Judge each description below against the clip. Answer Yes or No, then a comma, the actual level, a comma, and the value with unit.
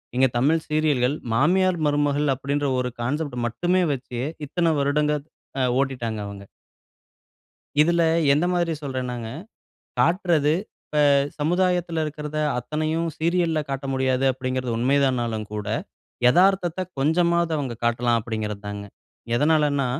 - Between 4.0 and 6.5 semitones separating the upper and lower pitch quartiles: Yes, average, 4.5 semitones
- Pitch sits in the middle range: Yes, medium, 145 Hz